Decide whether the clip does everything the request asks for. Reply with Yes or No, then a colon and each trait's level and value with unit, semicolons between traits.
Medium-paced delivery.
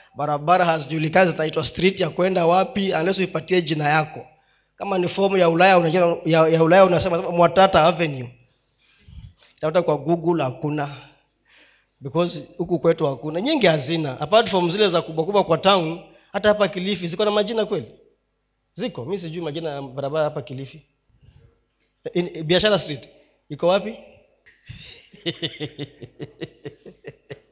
Yes: average, 130 wpm